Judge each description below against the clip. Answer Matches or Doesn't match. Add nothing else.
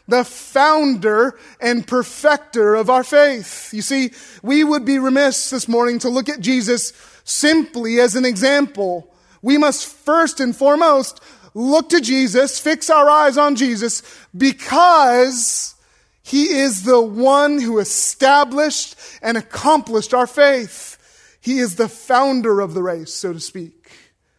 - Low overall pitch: Doesn't match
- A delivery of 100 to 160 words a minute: Matches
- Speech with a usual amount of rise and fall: Matches